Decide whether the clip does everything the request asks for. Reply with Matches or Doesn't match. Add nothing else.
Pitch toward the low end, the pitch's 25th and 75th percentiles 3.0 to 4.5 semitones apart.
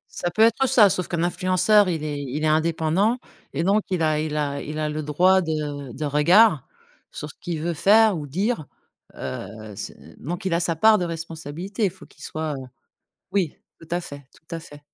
Doesn't match